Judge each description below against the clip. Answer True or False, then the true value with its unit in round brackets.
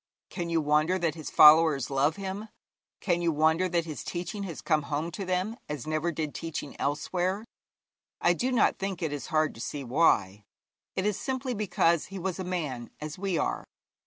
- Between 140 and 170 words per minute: False (190 wpm)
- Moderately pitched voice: True (165 Hz)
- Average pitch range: True (3.6 semitones)